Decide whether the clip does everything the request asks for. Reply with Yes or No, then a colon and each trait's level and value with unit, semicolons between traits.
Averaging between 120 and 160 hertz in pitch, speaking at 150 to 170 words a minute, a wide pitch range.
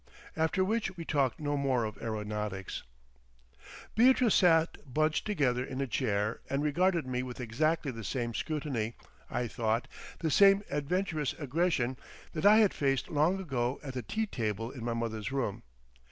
Yes: medium, 140 Hz; average, 160 wpm; wide, 5.7 semitones